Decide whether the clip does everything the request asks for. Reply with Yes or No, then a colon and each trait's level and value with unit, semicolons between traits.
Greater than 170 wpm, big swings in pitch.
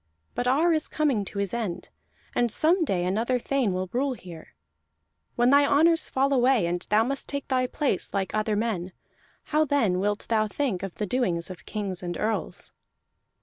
Yes: average, 185 wpm; wide, 6.4 semitones